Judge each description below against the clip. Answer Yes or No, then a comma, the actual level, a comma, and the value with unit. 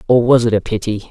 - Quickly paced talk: Yes, fast, 270 wpm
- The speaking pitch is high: No, low, 115 Hz